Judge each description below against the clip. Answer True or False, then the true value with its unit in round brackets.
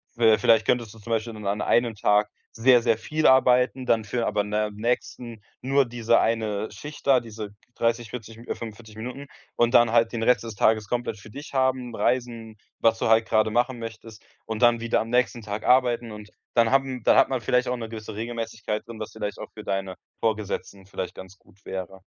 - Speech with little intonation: True (2.2 semitones)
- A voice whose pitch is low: True (115 Hz)